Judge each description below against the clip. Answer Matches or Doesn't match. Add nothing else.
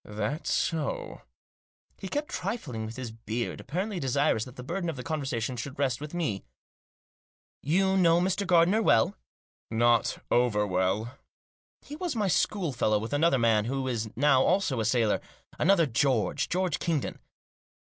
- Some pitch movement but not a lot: Doesn't match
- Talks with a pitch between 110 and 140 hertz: Matches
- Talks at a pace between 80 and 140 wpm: Doesn't match